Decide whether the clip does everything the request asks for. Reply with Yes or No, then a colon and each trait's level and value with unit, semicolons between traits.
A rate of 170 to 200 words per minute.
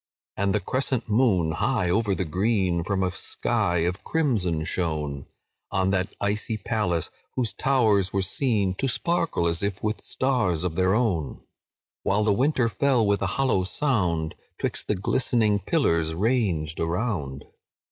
No: average, 150 wpm